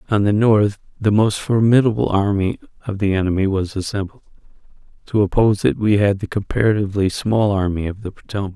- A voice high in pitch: No, low, 100 Hz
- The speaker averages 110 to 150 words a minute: No, average, 170 wpm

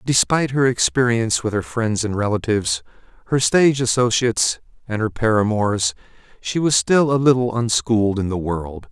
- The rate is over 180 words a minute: No, average, 155 wpm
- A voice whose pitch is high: No, low, 115 Hz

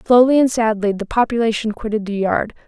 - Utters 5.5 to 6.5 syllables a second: Yes, 5.9 syllables/s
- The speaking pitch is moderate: No, high, 210 Hz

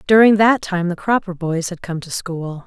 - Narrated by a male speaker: No, female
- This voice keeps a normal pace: No, fast, 225 wpm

